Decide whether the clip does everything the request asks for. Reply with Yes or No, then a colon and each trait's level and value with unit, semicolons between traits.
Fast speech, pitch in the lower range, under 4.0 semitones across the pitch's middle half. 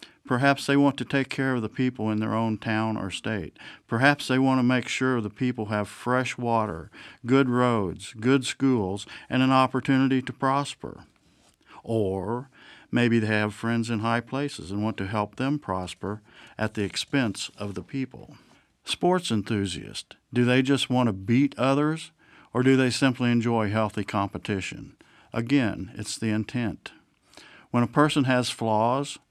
No: average, 165 wpm; low, 120 Hz; average, 3.6 semitones